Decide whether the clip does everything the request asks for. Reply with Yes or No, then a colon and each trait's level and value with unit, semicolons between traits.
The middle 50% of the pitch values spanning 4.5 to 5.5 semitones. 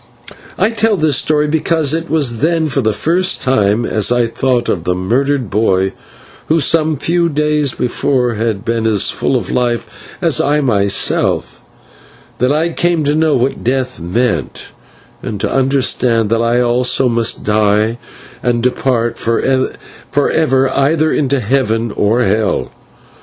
Yes: average, 4.8 semitones